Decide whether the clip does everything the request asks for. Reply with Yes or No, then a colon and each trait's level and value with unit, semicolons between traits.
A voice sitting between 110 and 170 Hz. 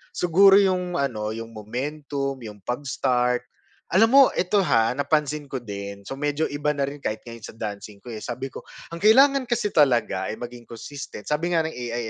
Yes: medium, 140 Hz